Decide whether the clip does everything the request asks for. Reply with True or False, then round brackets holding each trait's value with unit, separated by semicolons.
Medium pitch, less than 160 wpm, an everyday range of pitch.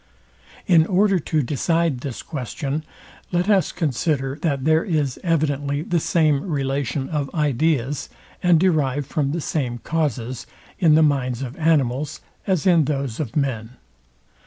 True (150 Hz; 140 wpm; 3.3 semitones)